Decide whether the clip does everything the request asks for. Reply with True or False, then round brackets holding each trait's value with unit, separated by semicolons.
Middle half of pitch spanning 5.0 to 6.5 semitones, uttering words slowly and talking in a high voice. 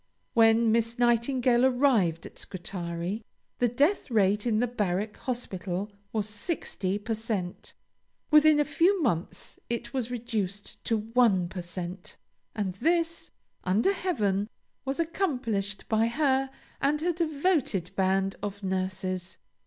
True (5.5 semitones; 130 wpm; 225 Hz)